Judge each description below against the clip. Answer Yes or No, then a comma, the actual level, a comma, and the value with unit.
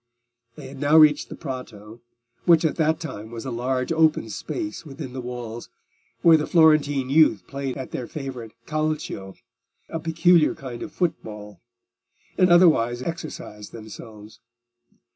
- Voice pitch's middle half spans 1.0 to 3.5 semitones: No, wide, 5.6 semitones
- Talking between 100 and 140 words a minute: Yes, slow, 135 wpm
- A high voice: No, low, 135 Hz